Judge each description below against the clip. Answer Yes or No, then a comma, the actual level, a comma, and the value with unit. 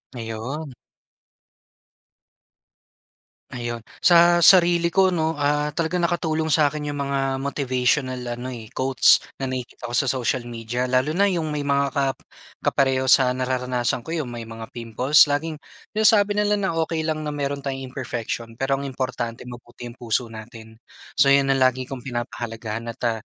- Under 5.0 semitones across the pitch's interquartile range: Yes, average, 3.9 semitones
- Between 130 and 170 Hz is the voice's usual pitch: Yes, low, 135 Hz